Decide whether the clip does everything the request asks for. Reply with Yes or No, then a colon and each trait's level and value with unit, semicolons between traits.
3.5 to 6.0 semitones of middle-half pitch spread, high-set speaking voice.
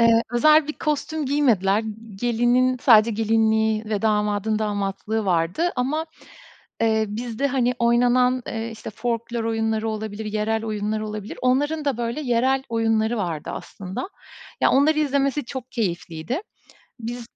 No: average, 2.9 semitones; high, 230 Hz